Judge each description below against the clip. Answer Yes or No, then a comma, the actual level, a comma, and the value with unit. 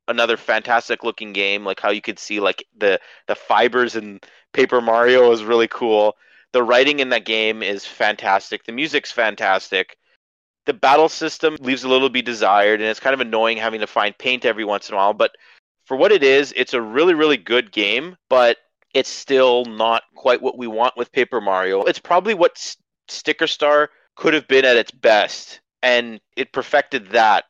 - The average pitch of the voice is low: Yes, low, 120 Hz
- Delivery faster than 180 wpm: Yes, average, 195 wpm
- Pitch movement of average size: Yes, average, 3.4 semitones